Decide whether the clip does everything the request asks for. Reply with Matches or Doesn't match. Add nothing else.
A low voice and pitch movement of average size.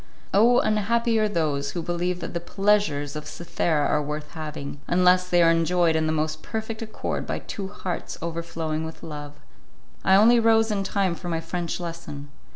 Doesn't match